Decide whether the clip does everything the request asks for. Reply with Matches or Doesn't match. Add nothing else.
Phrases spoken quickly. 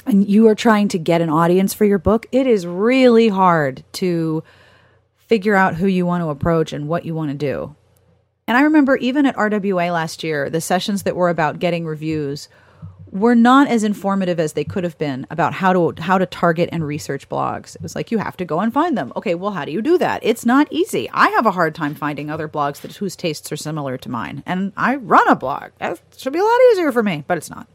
Matches